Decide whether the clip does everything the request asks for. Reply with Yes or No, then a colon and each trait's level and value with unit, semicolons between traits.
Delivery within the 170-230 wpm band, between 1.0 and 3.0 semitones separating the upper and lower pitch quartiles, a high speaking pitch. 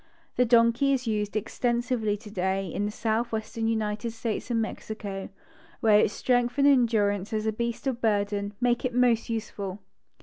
No: average, 160 wpm; narrow, 2.4 semitones; high, 225 Hz